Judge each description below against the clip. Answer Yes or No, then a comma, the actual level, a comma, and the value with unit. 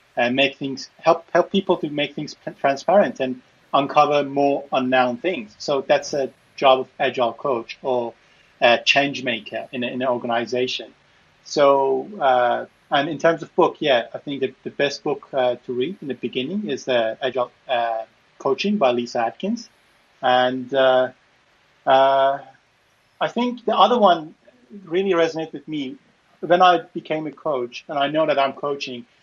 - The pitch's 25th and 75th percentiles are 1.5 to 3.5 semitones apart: No, average, 4.1 semitones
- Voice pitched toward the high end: No, medium, 140 Hz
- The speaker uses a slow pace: No, average, 170 wpm